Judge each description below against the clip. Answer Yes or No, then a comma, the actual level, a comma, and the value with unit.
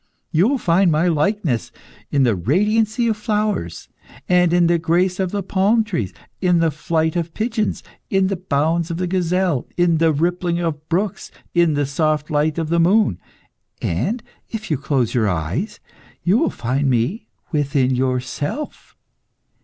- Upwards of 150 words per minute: Yes, average, 160 wpm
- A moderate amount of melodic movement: Yes, average, 4.7 semitones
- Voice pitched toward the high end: No, medium, 170 Hz